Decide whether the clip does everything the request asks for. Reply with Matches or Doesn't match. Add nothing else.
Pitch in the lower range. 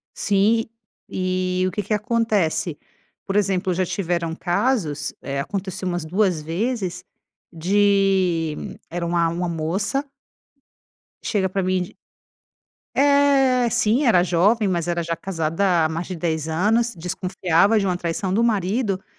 Doesn't match